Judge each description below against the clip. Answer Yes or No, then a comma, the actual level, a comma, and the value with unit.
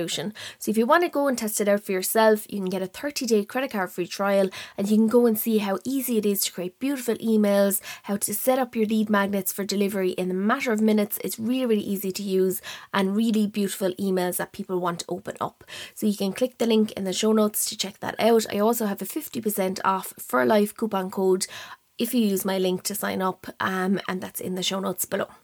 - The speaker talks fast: Yes, fast, 250 wpm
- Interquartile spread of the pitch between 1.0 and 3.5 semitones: Yes, average, 2.7 semitones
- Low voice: No, high, 205 Hz